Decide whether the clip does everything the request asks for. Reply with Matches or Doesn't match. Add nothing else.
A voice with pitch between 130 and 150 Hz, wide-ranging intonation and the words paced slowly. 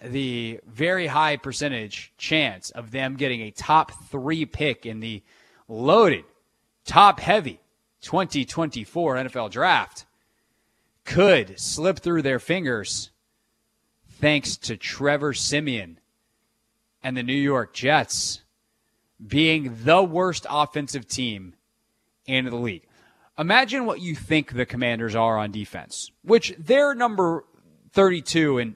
Matches